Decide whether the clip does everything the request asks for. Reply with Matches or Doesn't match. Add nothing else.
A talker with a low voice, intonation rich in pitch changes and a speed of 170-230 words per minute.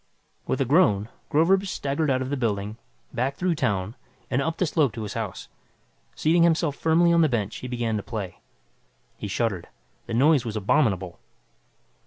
Matches